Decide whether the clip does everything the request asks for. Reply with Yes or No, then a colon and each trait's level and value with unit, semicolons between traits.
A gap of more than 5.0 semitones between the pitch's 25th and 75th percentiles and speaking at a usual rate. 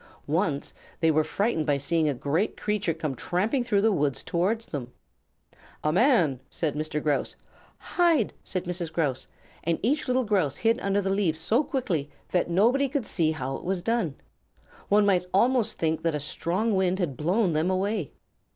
Yes: wide, 5.6 semitones; average, 180 wpm